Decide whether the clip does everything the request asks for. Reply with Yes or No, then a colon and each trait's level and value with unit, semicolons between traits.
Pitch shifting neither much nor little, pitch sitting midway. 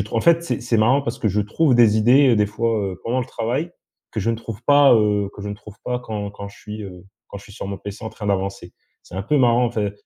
No: average, 3.2 semitones; low, 110 Hz